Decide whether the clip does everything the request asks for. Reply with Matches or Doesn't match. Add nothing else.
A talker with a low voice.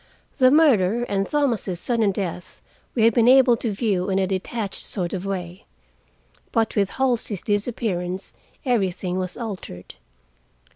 Doesn't match